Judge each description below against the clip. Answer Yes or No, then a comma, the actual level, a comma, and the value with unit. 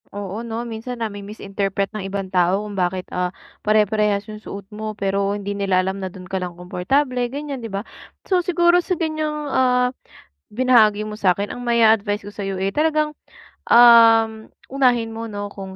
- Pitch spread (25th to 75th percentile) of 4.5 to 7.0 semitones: No, average, 3.8 semitones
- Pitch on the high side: Yes, high, 215 Hz